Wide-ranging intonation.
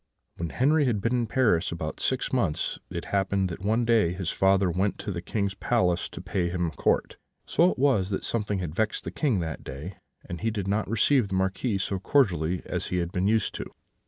No: average, 4.1 semitones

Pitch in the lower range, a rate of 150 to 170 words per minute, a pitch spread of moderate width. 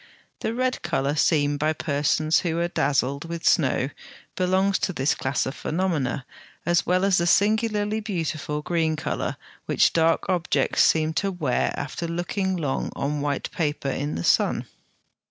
No: medium, 160 Hz; average, 155 wpm; average, 4.0 semitones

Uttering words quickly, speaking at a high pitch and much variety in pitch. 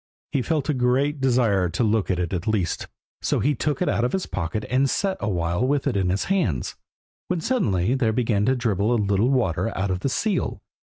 No: fast, 225 wpm; low, 115 Hz; wide, 5.9 semitones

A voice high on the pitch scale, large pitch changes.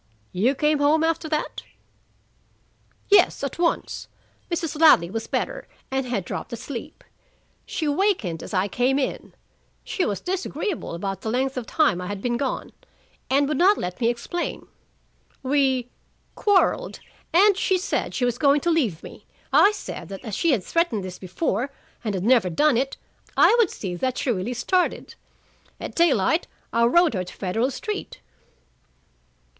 Yes: very high, 265 Hz; wide, 7.0 semitones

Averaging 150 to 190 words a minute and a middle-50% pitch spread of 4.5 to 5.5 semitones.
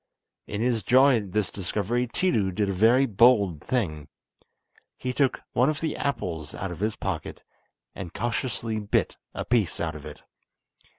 Yes: average, 165 wpm; average, 4.8 semitones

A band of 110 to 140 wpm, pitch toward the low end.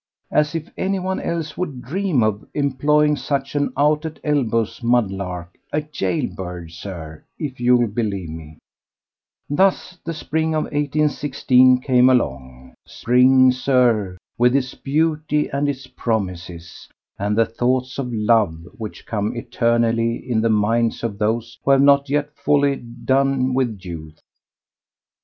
Yes: slow, 135 wpm; low, 125 Hz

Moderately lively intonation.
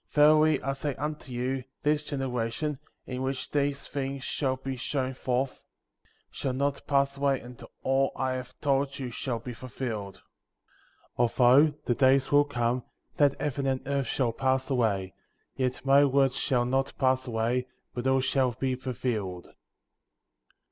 No: narrow, 1.8 semitones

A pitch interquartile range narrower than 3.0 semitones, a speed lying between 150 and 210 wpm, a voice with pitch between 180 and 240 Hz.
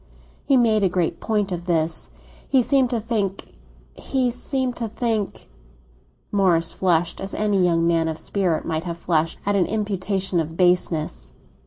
No: average, 4.5 semitones; average, 155 wpm; medium, 185 Hz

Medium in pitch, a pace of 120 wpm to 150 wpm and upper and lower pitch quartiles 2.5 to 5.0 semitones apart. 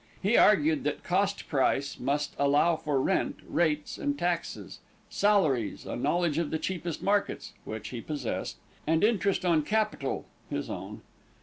No: medium, 165 Hz; average, 145 wpm; wide, 5.6 semitones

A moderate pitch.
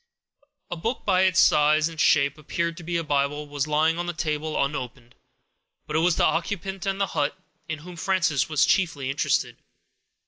Yes: medium, 160 Hz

